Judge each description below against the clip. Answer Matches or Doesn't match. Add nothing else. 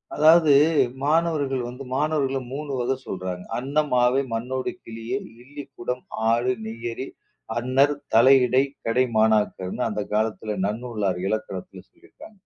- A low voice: Matches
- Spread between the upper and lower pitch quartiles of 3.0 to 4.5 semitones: Matches